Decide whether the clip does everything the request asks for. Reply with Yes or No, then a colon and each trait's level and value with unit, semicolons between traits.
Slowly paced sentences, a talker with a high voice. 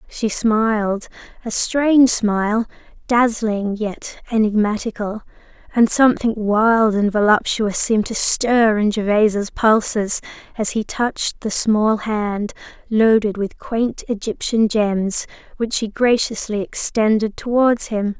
Yes: slow, 110 wpm; high, 220 Hz